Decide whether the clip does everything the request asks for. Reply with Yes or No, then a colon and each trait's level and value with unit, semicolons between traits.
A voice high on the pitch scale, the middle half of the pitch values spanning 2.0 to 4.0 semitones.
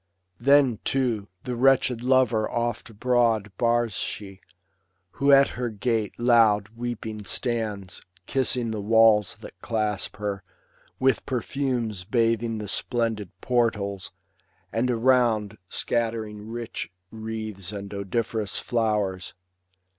No: low, 115 Hz; narrow, 2.4 semitones